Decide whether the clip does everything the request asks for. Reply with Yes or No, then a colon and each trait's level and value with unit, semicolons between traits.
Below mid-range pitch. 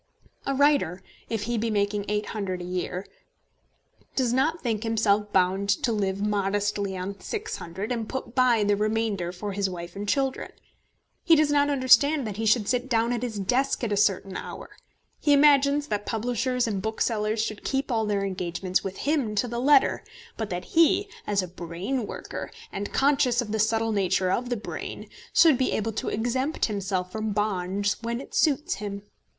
No: high, 215 Hz